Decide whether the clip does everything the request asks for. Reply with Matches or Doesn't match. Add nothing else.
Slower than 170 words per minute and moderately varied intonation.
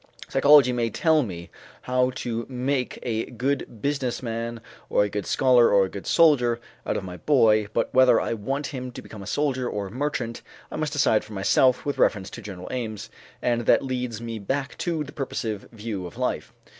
Doesn't match